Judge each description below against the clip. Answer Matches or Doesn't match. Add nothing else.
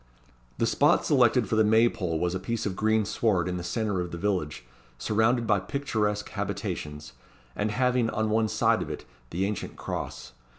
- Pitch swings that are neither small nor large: Matches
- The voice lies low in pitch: Matches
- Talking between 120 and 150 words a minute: Doesn't match